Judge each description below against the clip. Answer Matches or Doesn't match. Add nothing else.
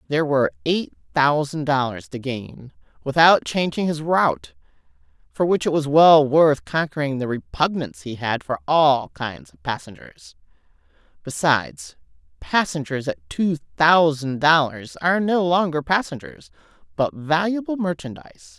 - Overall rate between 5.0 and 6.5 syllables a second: Doesn't match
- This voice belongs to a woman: Matches